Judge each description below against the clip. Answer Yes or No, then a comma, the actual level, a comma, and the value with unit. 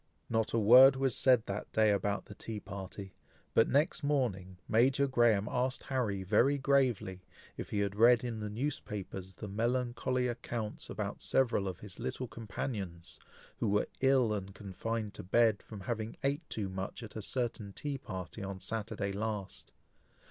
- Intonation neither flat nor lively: Yes, average, 4.0 semitones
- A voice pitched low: Yes, low, 110 Hz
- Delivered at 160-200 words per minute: Yes, average, 165 wpm